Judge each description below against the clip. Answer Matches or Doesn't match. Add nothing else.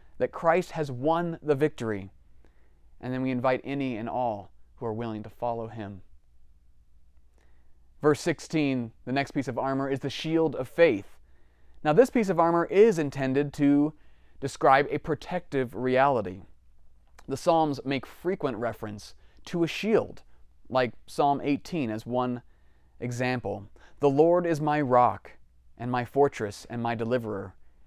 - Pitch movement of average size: Doesn't match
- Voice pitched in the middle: Doesn't match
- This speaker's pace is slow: Doesn't match